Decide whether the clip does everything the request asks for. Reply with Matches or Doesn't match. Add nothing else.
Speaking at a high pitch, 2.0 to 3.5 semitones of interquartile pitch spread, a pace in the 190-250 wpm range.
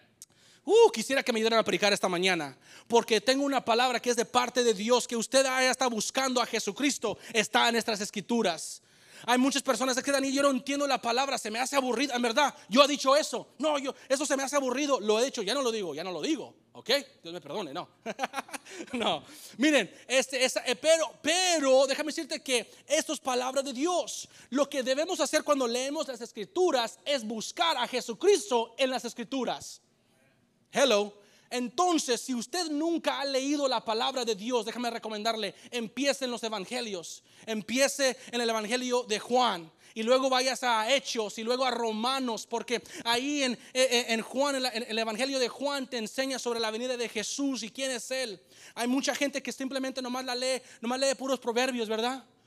Matches